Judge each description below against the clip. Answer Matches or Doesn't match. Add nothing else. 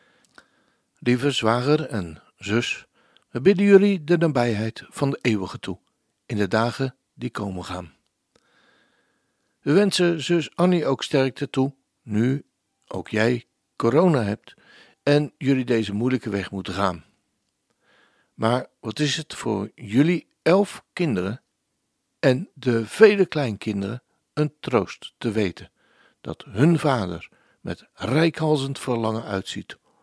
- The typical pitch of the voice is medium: Doesn't match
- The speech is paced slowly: Matches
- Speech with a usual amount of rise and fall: Doesn't match